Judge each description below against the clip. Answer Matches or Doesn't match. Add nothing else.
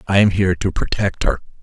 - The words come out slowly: Doesn't match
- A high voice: Doesn't match